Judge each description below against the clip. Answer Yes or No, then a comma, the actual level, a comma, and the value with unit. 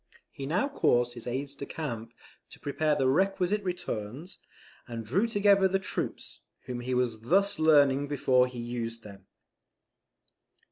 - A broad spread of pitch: Yes, wide, 7.0 semitones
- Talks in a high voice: No, medium, 140 Hz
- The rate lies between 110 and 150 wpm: Yes, average, 145 wpm